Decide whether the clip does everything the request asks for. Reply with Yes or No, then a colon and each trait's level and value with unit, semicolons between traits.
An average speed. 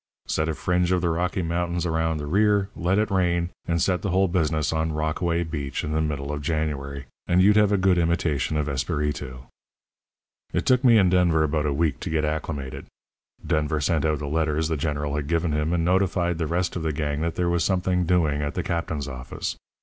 No: fast, 215 wpm